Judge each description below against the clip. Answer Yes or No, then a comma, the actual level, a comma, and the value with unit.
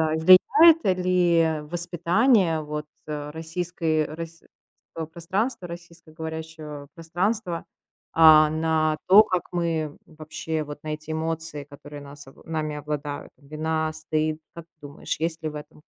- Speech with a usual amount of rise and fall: No, narrow, 1.9 semitones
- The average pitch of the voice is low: No, medium, 160 Hz